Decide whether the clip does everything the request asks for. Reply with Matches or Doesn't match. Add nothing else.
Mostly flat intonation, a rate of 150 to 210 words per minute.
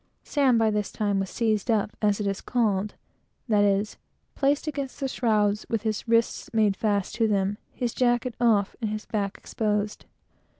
Matches